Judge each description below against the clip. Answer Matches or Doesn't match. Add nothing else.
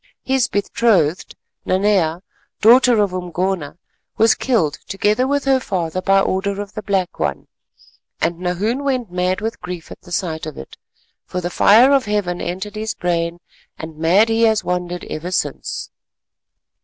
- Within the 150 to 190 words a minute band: Matches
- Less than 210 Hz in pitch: Matches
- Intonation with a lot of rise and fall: Doesn't match